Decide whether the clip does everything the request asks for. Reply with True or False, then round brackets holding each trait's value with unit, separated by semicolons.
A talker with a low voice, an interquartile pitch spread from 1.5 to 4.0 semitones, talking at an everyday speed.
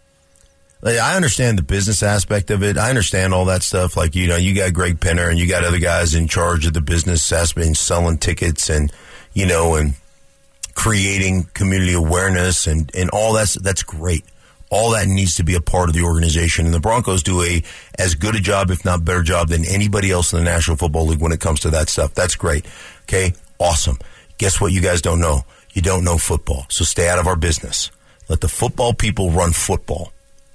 False (90 Hz; 2.5 semitones; 215 wpm)